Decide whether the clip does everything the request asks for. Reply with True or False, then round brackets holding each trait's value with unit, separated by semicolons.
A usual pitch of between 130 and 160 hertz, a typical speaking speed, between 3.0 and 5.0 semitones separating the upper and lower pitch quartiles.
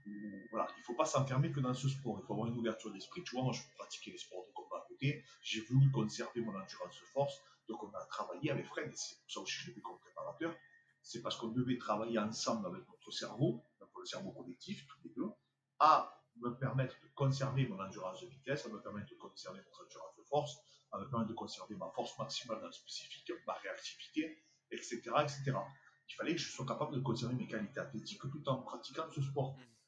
False (135 Hz; 225 wpm; 3.9 semitones)